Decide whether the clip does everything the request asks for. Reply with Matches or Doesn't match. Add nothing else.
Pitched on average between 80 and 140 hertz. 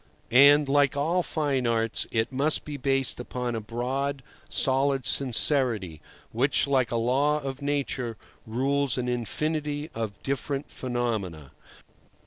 Matches